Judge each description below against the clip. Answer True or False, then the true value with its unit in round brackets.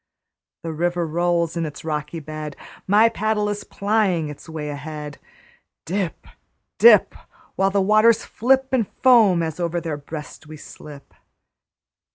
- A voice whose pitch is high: False (170 Hz)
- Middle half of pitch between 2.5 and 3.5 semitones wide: False (5.1 semitones)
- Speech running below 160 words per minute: True (140 wpm)